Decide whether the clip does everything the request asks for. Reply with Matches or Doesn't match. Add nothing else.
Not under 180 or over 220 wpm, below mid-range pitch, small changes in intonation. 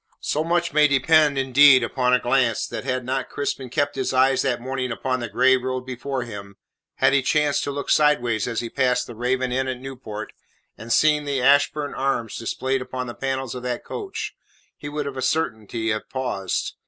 Matches